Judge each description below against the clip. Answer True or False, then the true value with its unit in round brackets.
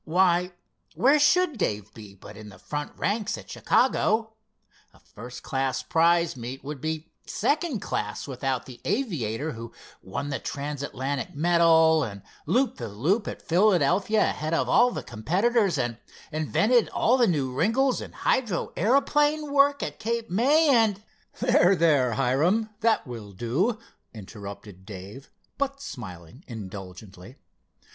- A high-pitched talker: False (160 Hz)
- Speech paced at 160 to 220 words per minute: False (140 wpm)